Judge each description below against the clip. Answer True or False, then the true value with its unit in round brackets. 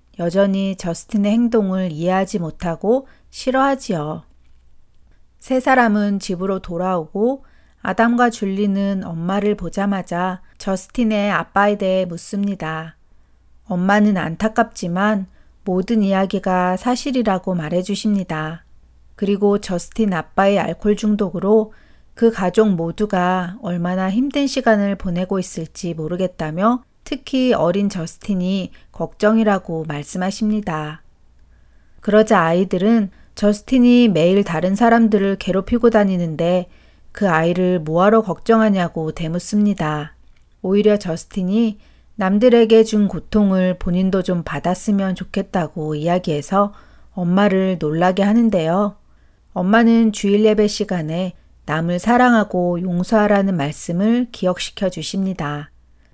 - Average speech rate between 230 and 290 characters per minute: True (280 characters per minute)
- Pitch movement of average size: True (3.4 semitones)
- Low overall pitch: False (190 Hz)